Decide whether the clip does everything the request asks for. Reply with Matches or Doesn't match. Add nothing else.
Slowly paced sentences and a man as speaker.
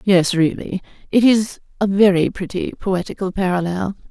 Doesn't match